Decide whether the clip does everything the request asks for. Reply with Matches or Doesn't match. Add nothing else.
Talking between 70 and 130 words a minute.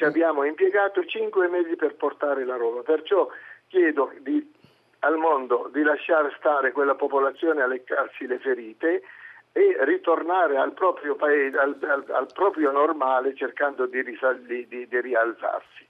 Doesn't match